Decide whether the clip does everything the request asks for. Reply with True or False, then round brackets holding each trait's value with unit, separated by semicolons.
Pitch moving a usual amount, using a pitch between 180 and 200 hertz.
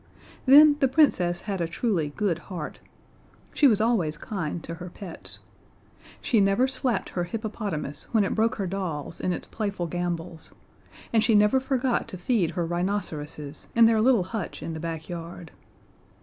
True (4.9 semitones; 190 Hz)